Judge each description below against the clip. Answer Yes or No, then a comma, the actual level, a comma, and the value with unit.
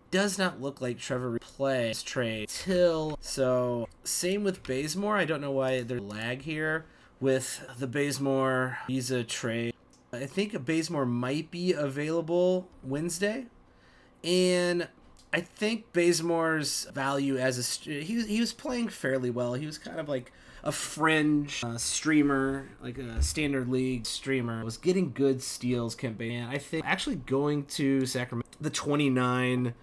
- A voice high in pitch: No, medium, 140 Hz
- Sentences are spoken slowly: No, average, 150 wpm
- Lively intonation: No, average, 4.8 semitones